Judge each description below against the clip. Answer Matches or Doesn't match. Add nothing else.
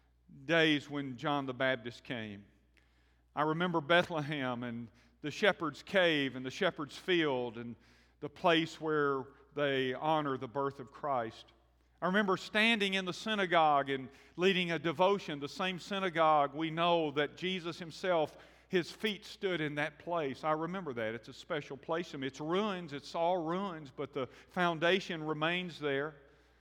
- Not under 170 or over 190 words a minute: Doesn't match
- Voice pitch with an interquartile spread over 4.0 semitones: Matches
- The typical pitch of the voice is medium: Matches